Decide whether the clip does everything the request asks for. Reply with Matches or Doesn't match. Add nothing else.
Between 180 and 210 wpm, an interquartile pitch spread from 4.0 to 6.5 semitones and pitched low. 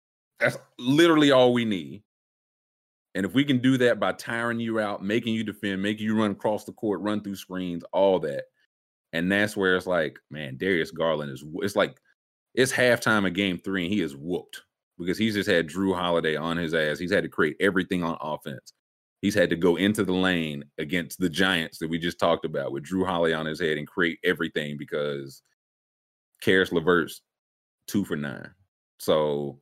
Matches